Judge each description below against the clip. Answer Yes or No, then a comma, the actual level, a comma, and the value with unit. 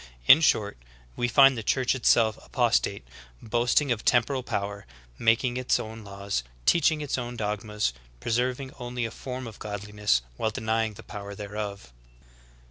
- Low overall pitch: Yes, low, 115 Hz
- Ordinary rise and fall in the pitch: Yes, average, 3.2 semitones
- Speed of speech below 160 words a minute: Yes, average, 150 wpm